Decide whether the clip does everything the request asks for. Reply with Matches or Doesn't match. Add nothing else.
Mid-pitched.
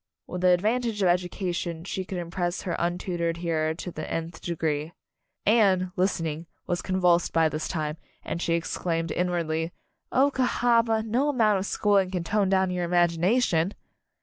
Matches